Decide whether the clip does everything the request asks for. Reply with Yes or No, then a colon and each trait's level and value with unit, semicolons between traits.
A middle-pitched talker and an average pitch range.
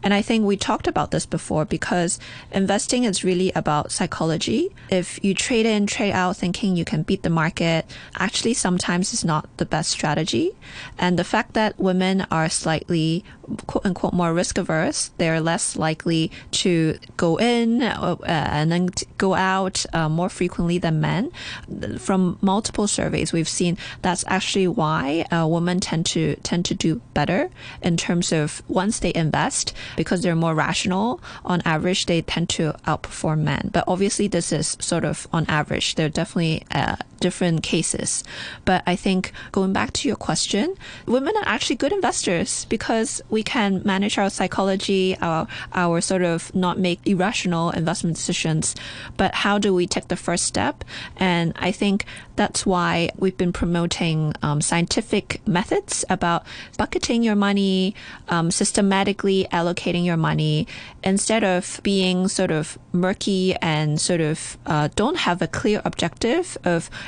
Yes: medium, 180 Hz; average, 3.0 semitones